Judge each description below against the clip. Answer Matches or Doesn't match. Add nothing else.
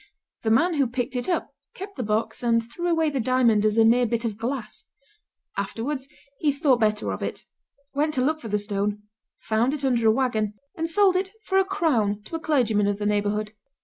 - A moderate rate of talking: Doesn't match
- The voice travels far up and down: Matches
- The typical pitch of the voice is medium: Doesn't match